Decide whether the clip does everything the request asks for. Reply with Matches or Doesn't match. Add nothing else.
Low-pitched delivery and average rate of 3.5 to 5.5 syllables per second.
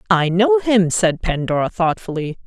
Doesn't match